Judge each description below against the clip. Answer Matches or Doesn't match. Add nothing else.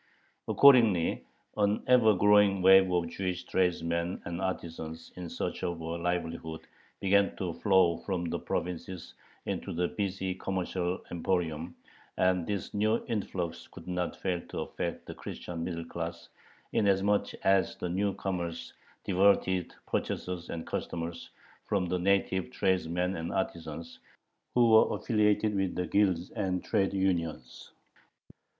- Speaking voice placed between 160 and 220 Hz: Doesn't match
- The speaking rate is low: Matches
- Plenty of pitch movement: Doesn't match